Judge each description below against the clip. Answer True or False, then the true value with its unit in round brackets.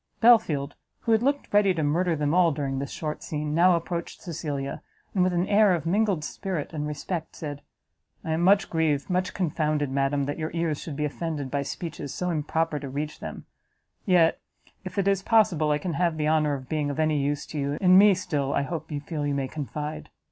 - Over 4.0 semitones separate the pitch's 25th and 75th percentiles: False (3.6 semitones)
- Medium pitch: True (155 Hz)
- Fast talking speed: True (215 wpm)